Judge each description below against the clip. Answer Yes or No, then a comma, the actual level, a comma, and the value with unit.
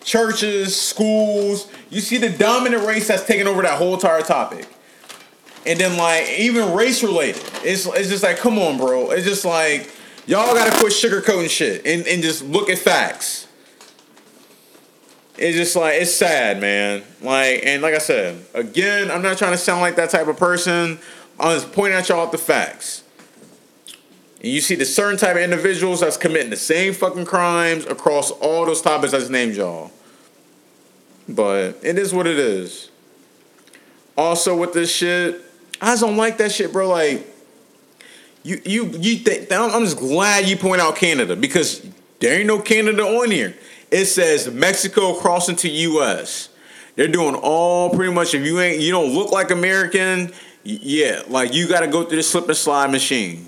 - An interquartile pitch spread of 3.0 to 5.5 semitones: Yes, average, 3.9 semitones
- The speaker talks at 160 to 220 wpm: Yes, average, 175 wpm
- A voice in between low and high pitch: Yes, medium, 180 Hz